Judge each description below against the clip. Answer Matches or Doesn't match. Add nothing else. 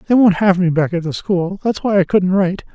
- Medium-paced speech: Doesn't match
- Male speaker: Matches